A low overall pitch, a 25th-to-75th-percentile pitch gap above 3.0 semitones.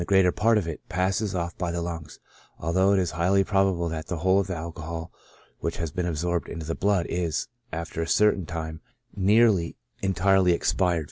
No: very low, 85 Hz; narrow, 2.6 semitones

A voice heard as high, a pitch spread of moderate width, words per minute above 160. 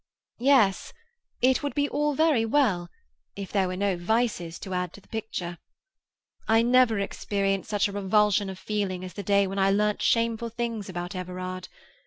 Yes: high, 200 Hz; average, 3.7 semitones; average, 175 wpm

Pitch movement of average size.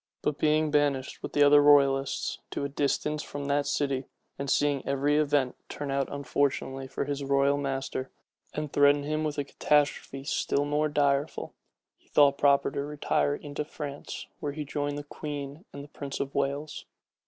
No: narrow, 1.0 semitones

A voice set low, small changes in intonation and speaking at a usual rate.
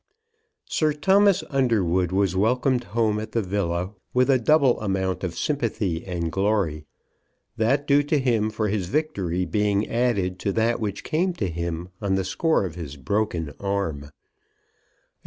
No: low, 105 Hz; average, 5.3 semitones; average, 155 wpm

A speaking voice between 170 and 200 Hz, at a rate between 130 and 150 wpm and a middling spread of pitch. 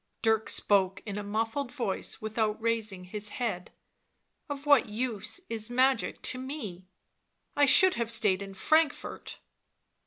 No: high, 220 Hz; slow, 135 wpm; average, 4.0 semitones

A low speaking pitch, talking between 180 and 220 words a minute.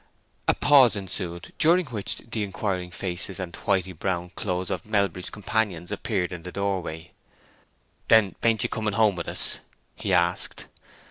No: very low, 95 Hz; average, 155 wpm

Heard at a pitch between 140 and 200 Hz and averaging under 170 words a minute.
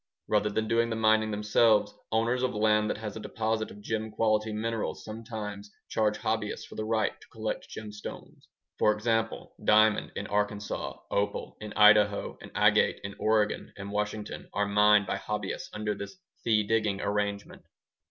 No: low, 105 Hz; average, 160 wpm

